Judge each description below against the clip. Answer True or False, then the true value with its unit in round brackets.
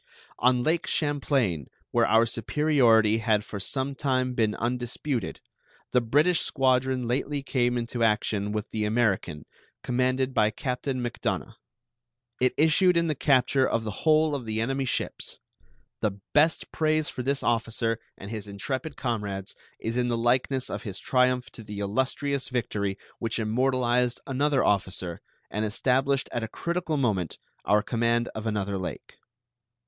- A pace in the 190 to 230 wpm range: False (150 wpm)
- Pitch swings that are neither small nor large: True (3.7 semitones)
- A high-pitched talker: False (120 Hz)